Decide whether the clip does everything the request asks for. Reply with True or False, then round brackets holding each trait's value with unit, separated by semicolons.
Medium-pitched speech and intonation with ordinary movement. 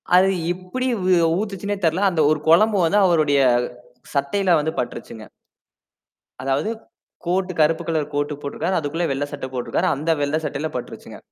True (160 Hz; 4.3 semitones)